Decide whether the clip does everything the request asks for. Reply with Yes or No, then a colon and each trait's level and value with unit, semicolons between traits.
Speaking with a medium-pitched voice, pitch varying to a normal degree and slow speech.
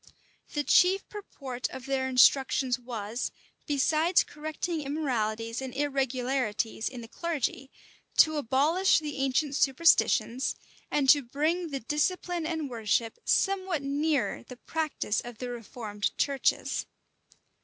No: very high, 275 Hz; average, 4.1 semitones; slow, 120 wpm